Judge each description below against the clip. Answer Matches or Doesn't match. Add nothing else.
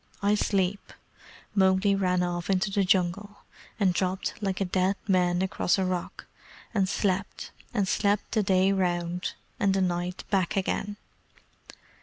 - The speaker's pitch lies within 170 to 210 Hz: Matches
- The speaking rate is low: Doesn't match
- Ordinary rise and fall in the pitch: Doesn't match